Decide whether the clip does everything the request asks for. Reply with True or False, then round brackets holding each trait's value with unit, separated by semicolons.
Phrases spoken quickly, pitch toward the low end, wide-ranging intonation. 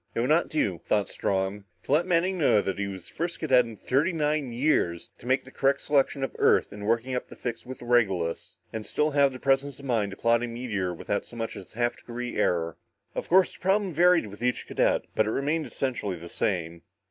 True (235 wpm; 120 Hz; 5.7 semitones)